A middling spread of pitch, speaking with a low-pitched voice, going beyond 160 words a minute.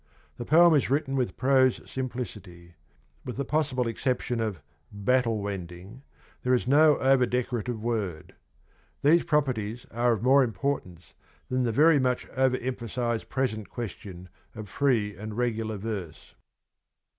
No: average, 3.7 semitones; low, 120 Hz; average, 145 wpm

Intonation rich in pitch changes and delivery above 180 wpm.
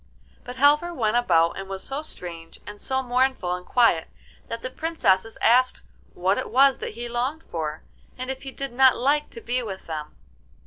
Yes: wide, 5.7 semitones; average, 190 wpm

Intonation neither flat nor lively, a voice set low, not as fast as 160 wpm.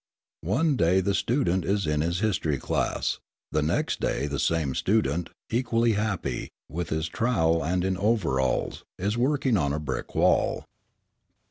No: wide, 5.9 semitones; very low, 90 Hz; average, 150 wpm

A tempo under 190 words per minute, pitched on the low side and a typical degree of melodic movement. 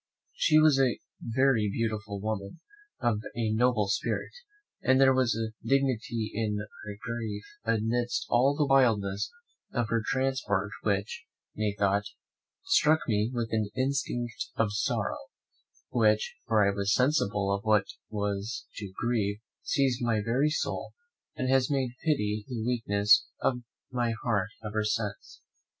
Yes: average, 140 wpm; low, 115 Hz; average, 3.5 semitones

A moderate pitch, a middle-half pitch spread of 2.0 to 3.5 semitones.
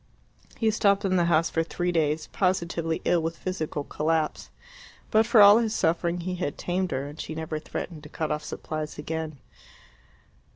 Yes: medium, 165 Hz; average, 2.9 semitones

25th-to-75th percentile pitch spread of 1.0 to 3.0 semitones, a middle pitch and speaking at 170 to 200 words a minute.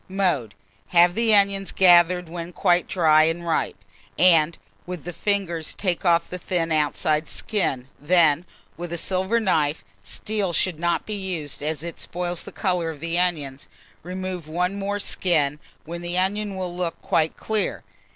No: average, 2.7 semitones; medium, 175 Hz; average, 160 wpm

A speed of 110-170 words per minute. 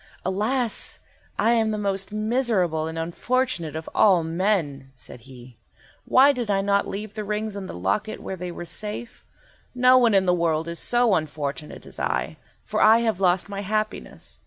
No: average, 180 wpm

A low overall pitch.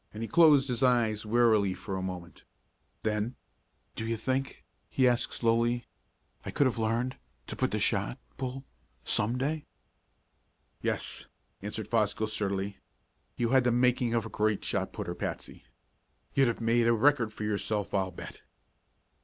Yes: low, 115 Hz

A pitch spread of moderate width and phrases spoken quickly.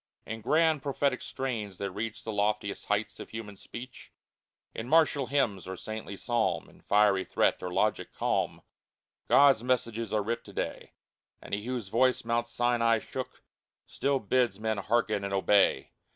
No: average, 3.5 semitones; average, 165 wpm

